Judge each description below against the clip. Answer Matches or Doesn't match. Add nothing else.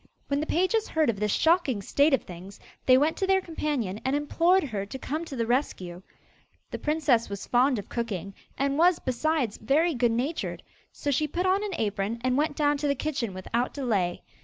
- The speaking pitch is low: Doesn't match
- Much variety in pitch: Matches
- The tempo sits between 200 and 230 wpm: Matches